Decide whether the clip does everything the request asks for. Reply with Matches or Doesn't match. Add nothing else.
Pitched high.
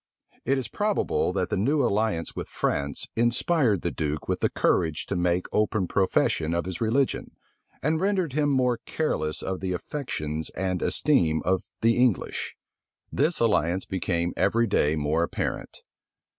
Doesn't match